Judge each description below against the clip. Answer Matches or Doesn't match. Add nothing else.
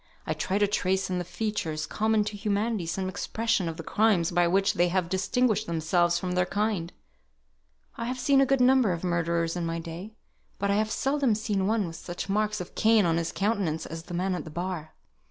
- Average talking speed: Doesn't match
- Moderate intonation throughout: Matches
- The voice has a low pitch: Doesn't match